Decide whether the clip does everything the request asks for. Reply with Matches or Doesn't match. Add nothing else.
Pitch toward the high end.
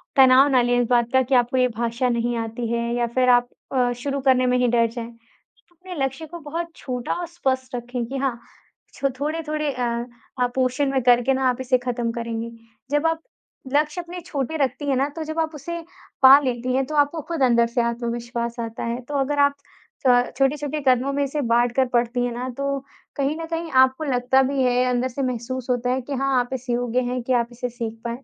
Matches